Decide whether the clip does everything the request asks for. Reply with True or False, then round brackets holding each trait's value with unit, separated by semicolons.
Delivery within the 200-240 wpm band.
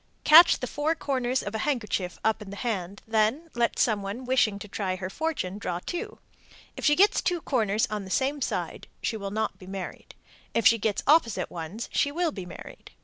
True (205 wpm)